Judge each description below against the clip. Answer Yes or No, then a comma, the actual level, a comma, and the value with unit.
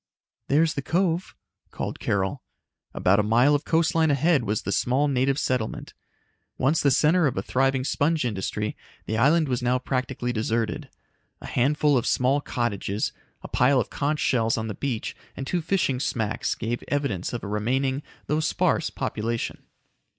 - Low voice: Yes, low, 130 Hz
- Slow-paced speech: No, average, 165 wpm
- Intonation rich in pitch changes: No, average, 4.5 semitones